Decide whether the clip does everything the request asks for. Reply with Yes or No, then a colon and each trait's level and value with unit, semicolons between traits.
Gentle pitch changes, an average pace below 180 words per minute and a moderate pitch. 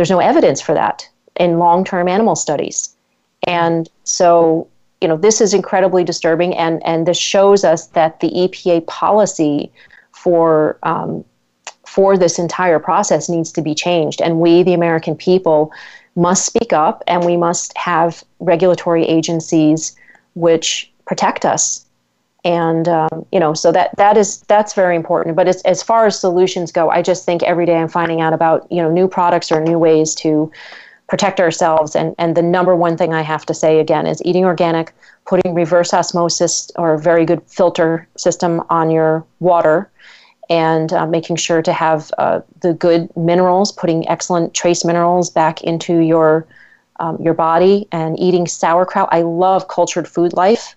Yes: narrow, 1.6 semitones; average, 170 wpm; medium, 170 Hz